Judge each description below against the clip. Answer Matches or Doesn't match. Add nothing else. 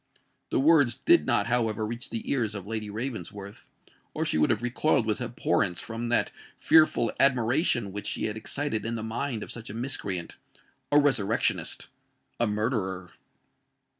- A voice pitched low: Matches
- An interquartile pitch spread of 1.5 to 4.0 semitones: Matches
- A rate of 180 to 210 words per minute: Doesn't match